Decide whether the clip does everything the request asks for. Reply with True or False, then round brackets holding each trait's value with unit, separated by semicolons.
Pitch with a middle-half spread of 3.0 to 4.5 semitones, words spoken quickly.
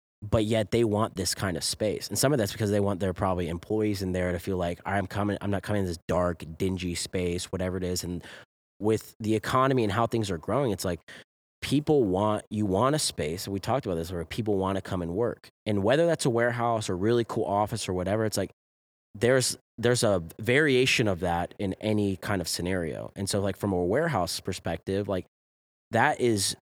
True (3.5 semitones; 220 wpm)